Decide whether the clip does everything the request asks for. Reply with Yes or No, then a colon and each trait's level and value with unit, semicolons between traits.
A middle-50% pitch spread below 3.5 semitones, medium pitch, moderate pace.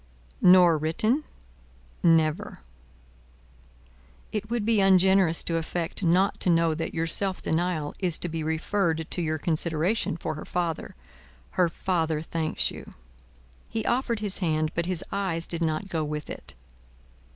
Yes: average, 3.0 semitones; medium, 170 Hz; average, 145 wpm